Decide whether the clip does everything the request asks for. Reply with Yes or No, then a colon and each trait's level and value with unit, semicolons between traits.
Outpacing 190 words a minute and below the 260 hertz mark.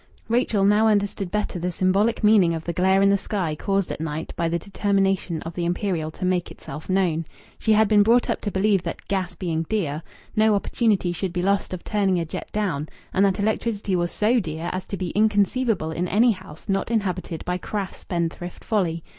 Yes: fast, 205 wpm; high, 190 Hz